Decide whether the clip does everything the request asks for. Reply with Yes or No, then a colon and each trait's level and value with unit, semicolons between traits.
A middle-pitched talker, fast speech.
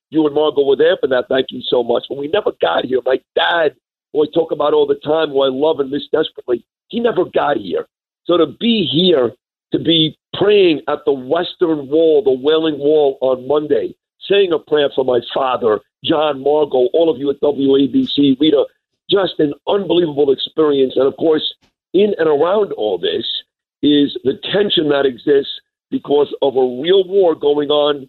No: medium, 160 Hz; average, 190 wpm